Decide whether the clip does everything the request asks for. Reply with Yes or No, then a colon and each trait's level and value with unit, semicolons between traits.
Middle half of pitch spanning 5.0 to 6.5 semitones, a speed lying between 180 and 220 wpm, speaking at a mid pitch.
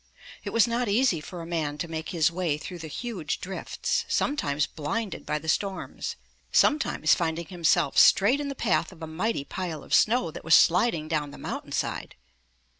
Yes: wide, 5.6 semitones; average, 190 wpm; medium, 170 Hz